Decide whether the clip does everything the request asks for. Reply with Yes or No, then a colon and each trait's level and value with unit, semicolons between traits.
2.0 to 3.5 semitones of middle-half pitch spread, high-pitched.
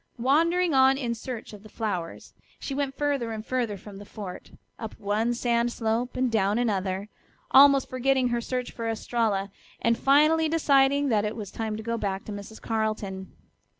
No: average, 4.0 semitones; high, 230 Hz